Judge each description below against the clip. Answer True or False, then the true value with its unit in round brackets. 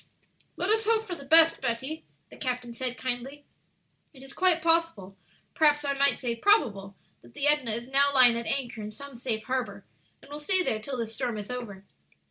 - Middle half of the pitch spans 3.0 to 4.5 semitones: True (4.2 semitones)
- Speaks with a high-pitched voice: True (260 Hz)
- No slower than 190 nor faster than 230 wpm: True (200 wpm)